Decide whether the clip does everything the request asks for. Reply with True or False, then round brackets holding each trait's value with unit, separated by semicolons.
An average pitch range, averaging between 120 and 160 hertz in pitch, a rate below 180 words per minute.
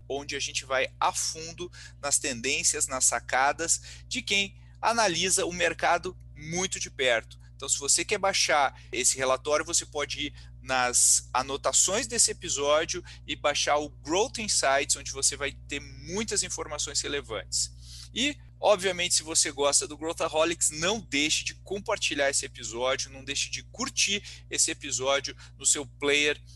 True (4.6 semitones; 140 Hz; 150 wpm)